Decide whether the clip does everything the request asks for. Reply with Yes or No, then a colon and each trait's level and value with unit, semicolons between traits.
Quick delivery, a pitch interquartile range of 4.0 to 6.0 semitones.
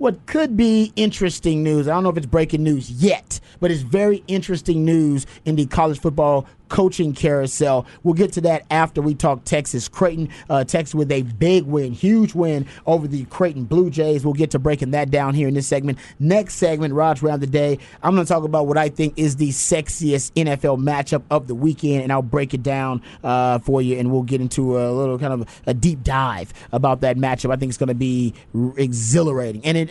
No: fast, 225 wpm; average, 3.6 semitones